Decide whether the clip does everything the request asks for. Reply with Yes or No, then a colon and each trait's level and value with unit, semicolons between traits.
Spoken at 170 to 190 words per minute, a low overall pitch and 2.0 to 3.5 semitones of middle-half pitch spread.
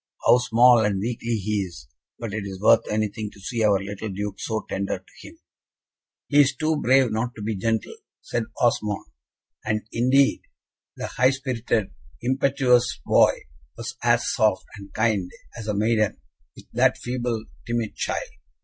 No: average, 160 wpm; low, 110 Hz; average, 3.0 semitones